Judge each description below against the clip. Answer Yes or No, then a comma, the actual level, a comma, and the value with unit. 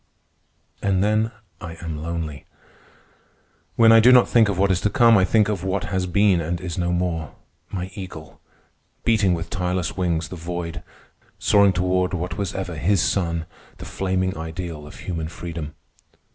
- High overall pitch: No, very low, 90 Hz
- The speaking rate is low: No, average, 165 wpm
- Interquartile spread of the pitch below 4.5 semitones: Yes, average, 2.8 semitones